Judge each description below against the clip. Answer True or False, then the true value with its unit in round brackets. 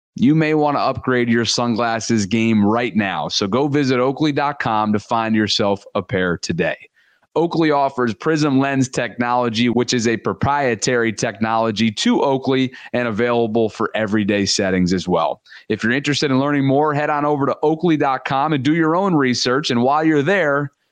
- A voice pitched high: False (125 Hz)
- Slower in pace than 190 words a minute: True (170 wpm)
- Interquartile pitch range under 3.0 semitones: False (4.4 semitones)